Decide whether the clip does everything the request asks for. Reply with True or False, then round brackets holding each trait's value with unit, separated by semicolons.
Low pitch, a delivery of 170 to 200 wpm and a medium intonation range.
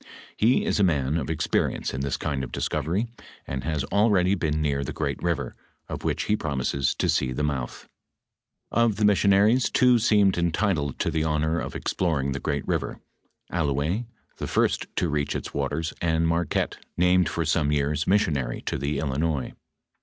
True (80 Hz; 180 wpm; 4.5 semitones)